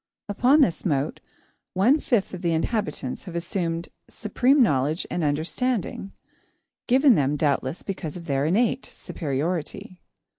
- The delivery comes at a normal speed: No, slow, 125 wpm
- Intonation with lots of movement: Yes, wide, 6.5 semitones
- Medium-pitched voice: Yes, medium, 175 Hz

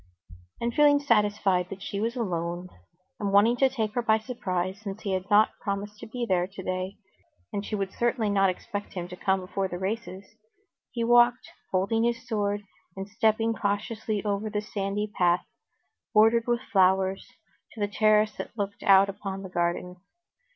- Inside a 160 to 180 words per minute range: Yes, average, 170 wpm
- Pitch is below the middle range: No, high, 205 Hz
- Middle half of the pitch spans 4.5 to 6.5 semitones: No, average, 2.7 semitones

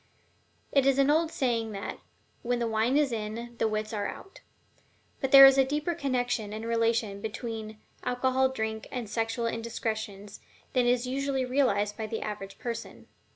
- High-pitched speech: Yes, high, 235 Hz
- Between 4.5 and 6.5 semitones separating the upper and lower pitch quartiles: No, average, 3.3 semitones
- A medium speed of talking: Yes, average, 165 wpm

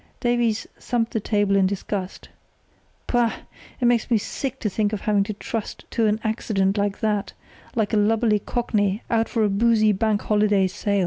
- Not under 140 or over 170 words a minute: No, average, 180 wpm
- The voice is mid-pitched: No, high, 215 Hz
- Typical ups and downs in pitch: No, narrow, 2.0 semitones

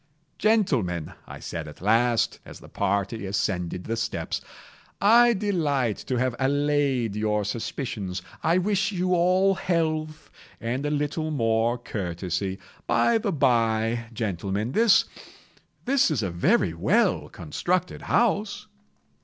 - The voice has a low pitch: Yes, low, 125 Hz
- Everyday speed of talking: No, slow, 120 wpm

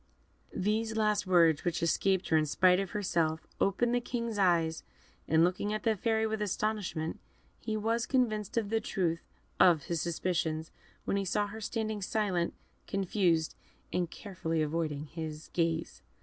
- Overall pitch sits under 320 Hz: Yes, medium, 185 Hz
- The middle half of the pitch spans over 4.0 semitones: Yes, average, 4.5 semitones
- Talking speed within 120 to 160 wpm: Yes, average, 155 wpm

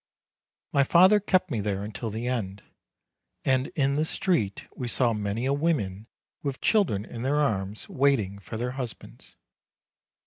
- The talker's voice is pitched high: No, low, 125 Hz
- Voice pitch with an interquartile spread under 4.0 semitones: No, average, 5.2 semitones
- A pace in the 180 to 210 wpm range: No, average, 145 wpm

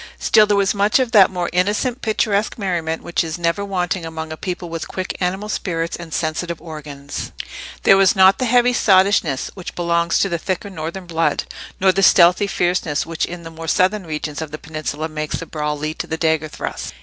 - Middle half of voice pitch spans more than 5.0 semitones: No, average, 3.3 semitones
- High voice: No, medium, 175 Hz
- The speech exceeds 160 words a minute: Yes, fast, 205 wpm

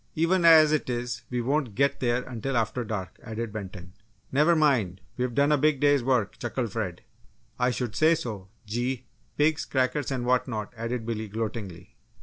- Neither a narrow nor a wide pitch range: Yes, average, 4.2 semitones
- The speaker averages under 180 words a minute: Yes, average, 170 wpm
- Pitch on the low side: Yes, low, 125 Hz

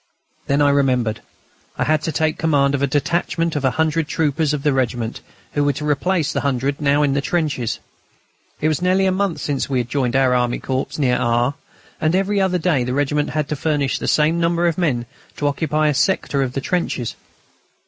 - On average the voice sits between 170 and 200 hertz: No, medium, 145 Hz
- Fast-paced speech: Yes, fast, 210 wpm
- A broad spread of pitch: No, average, 3.1 semitones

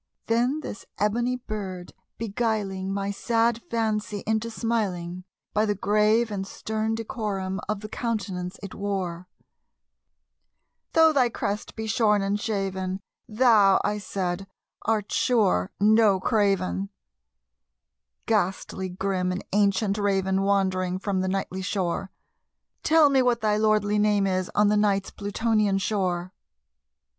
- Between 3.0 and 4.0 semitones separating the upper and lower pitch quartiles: No, narrow, 2.4 semitones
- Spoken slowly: Yes, slow, 125 wpm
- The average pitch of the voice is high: Yes, high, 205 Hz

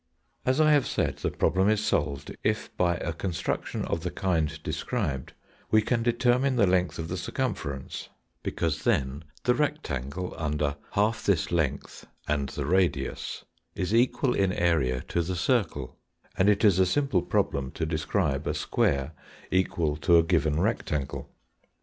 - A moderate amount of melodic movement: No, wide, 5.9 semitones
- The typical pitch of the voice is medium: No, very low, 85 Hz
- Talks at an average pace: Yes, average, 155 wpm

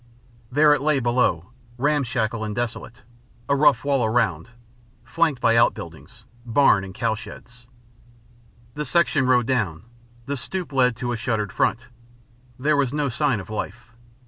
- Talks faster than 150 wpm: No, average, 145 wpm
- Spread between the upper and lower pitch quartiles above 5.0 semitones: No, average, 3.7 semitones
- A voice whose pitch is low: Yes, low, 125 Hz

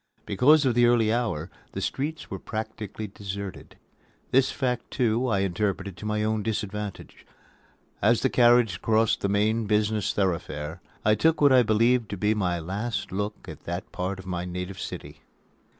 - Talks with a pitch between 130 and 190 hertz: No, low, 105 Hz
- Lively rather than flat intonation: No, average, 3.5 semitones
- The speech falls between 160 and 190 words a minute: Yes, average, 165 wpm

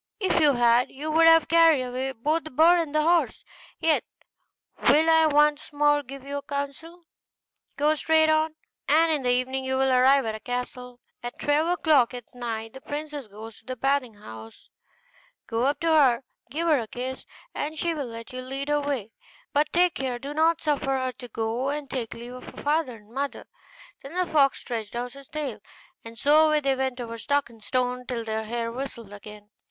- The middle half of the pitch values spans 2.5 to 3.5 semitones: No, average, 3.9 semitones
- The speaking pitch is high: Yes, very high, 270 Hz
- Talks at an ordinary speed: No, fast, 210 wpm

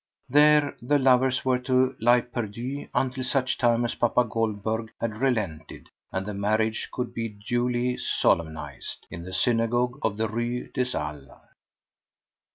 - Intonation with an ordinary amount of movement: Yes, average, 3.0 semitones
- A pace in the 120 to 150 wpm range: Yes, average, 145 wpm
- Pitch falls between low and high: No, low, 120 Hz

